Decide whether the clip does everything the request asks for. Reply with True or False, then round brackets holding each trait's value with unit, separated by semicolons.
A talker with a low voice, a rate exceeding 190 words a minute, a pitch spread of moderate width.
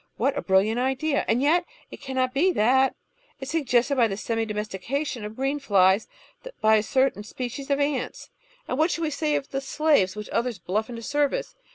False (260 Hz; 205 wpm; 4.6 semitones)